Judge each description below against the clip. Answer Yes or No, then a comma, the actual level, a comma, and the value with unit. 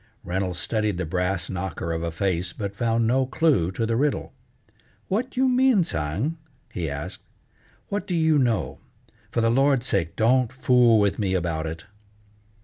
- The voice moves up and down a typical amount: No, wide, 7.2 semitones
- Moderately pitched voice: No, low, 110 Hz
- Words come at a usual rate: Yes, average, 165 wpm